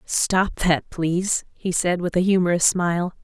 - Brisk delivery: No, average, 165 wpm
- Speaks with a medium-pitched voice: Yes, medium, 180 Hz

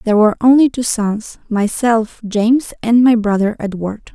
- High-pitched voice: Yes, high, 225 Hz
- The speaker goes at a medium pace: Yes, average, 160 wpm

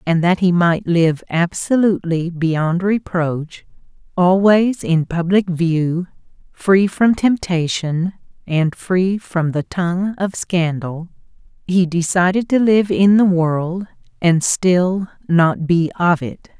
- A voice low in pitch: No, medium, 180 Hz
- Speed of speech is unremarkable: No, slow, 125 wpm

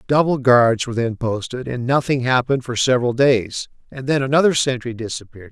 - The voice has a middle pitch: No, low, 125 Hz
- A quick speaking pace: No, average, 165 wpm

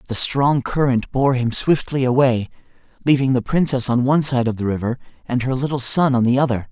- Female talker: No, male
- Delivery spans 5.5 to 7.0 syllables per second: Yes, 5.6 syllables/s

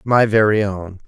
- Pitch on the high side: No, low, 105 Hz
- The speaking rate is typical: Yes, average, 170 wpm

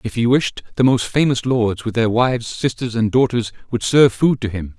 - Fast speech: Yes, fast, 225 wpm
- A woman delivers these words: No, male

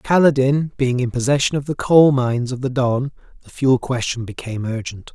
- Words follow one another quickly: No, average, 185 wpm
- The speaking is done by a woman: No, male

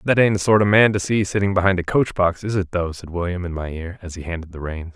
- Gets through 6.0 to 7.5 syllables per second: Yes, 6.3 syllables/s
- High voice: No, very low, 90 Hz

